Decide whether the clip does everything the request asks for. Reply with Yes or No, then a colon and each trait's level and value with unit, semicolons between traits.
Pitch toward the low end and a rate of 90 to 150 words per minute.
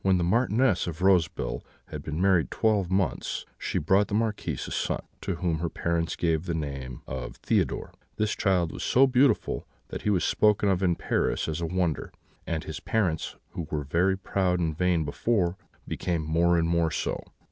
No: very low, 85 Hz; average, 190 wpm